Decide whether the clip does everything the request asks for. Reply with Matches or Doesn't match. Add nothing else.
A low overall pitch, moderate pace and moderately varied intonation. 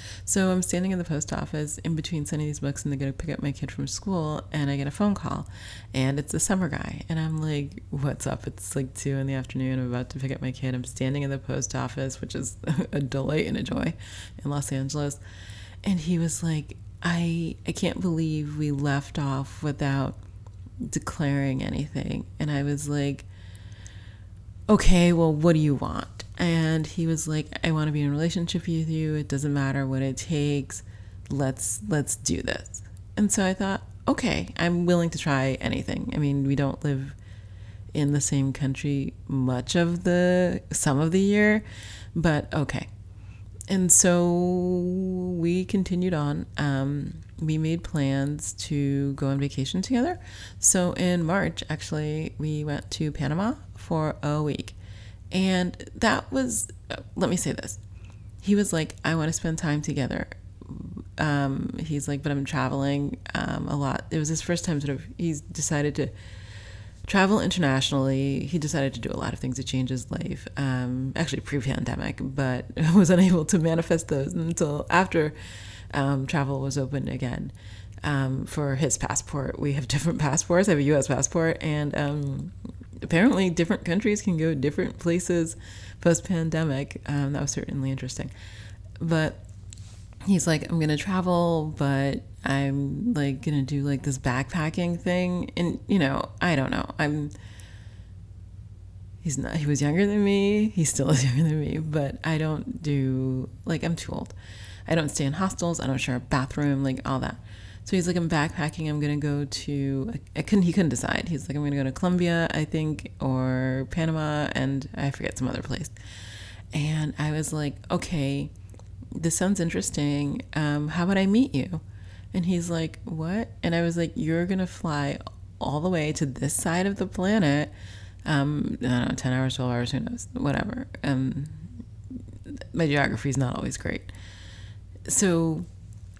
Doesn't match